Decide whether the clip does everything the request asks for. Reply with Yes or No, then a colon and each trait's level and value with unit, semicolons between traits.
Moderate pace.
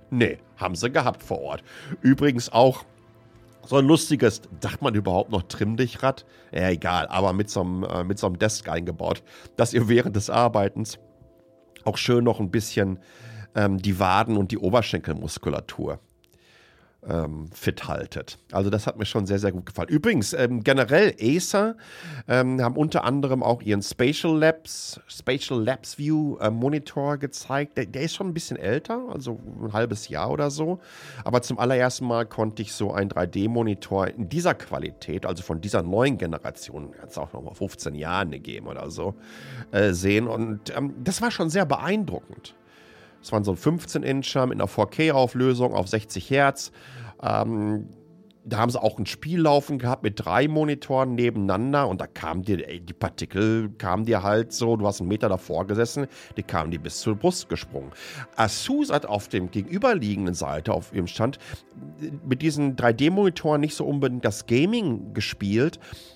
Yes: average, 170 wpm